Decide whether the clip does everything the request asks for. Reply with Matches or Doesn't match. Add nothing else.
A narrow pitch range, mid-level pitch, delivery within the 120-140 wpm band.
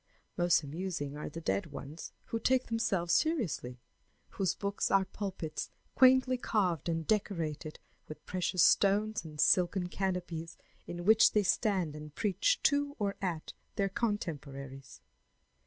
Doesn't match